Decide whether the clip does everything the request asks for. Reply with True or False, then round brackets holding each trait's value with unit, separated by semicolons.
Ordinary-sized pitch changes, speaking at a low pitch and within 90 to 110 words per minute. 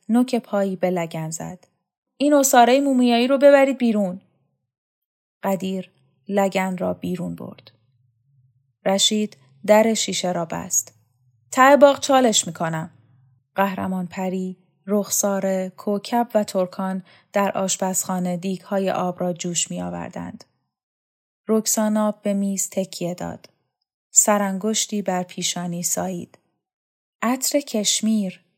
False (3.8 semitones; 190 Hz; 105 wpm)